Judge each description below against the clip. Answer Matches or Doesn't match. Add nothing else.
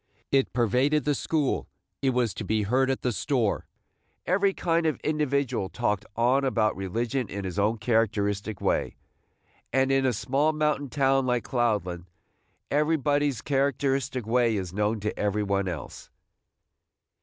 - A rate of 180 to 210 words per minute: Doesn't match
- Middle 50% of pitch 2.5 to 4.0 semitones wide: Doesn't match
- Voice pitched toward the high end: Doesn't match